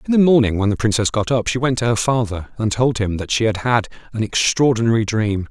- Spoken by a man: Yes, male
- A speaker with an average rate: No, fast, 250 wpm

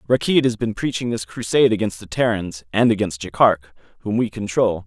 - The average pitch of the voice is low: Yes, low, 105 Hz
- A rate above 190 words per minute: No, average, 185 wpm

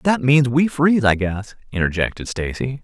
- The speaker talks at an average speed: Yes, average, 170 wpm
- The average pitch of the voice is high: No, low, 125 Hz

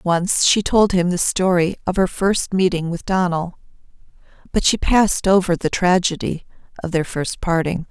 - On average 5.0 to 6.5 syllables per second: No, 4.6 syllables/s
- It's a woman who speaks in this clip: Yes, female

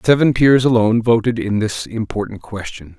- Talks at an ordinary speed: Yes, average, 160 wpm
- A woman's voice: No, male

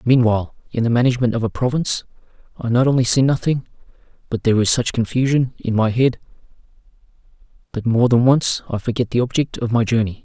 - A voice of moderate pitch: No, low, 120 Hz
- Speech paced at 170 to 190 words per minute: Yes, average, 180 wpm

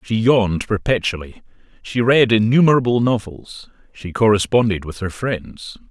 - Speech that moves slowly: Yes, slow, 120 wpm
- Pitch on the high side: No, low, 110 Hz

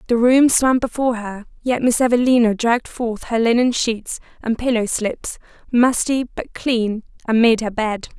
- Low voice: No, high, 235 Hz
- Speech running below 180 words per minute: Yes, average, 170 wpm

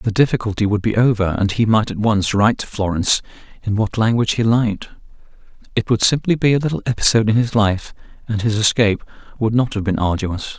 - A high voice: No, low, 110 Hz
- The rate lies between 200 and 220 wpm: Yes, fast, 205 wpm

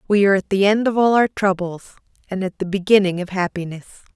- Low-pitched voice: No, high, 195 Hz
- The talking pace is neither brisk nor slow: No, fast, 215 wpm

